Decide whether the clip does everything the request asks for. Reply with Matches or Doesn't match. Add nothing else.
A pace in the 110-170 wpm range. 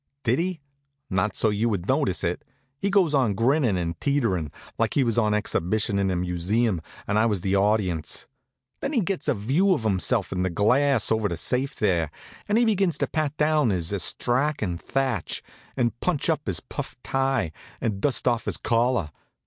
Doesn't match